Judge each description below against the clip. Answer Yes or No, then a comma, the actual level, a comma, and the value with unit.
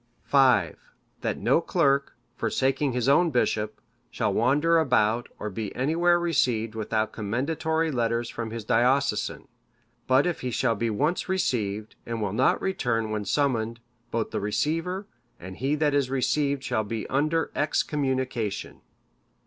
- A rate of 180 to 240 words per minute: No, average, 140 wpm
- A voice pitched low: Yes, low, 125 Hz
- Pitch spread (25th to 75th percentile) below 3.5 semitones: No, average, 4.7 semitones